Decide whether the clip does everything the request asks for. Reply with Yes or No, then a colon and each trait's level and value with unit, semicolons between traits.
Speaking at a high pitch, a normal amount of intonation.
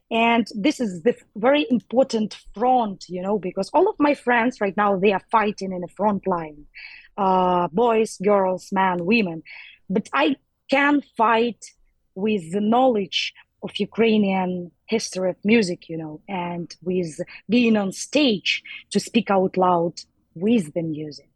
Yes: high, 205 Hz; average, 4.1 semitones